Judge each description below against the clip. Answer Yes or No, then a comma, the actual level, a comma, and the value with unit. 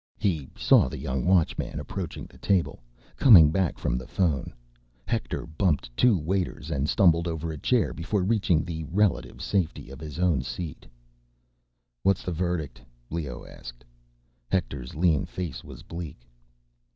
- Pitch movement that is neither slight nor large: Yes, average, 3.7 semitones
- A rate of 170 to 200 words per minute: No, average, 145 wpm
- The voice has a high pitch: No, very low, 85 Hz